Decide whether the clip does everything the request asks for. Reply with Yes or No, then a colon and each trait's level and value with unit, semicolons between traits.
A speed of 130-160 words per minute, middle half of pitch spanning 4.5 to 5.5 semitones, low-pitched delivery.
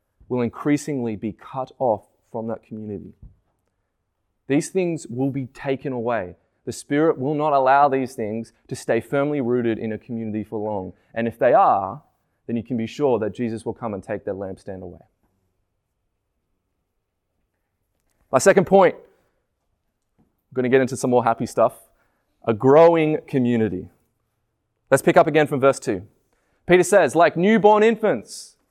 Yes: average, 155 wpm; average, 4.9 semitones; low, 115 Hz